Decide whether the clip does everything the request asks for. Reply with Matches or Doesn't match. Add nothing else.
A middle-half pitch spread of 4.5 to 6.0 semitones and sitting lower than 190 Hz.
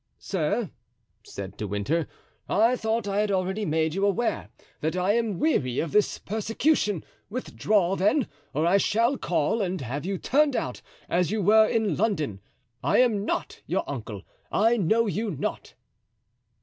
Doesn't match